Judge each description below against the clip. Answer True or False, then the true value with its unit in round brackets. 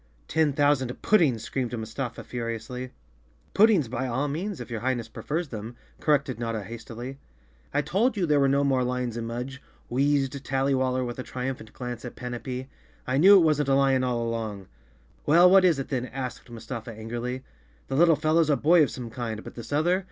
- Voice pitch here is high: False (130 Hz)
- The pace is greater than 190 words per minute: True (200 wpm)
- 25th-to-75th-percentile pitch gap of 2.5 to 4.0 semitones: True (3.5 semitones)